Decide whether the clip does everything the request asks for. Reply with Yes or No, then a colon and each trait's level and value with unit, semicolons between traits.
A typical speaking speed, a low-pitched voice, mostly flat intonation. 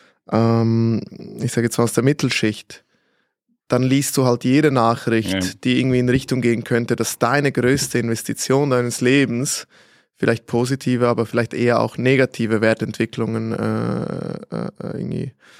Yes: average, 140 wpm; low, 120 Hz; narrow, 2.2 semitones